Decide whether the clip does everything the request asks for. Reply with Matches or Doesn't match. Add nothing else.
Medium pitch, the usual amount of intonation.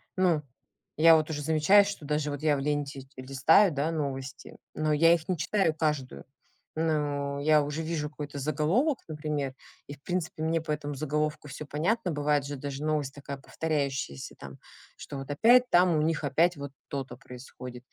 Doesn't match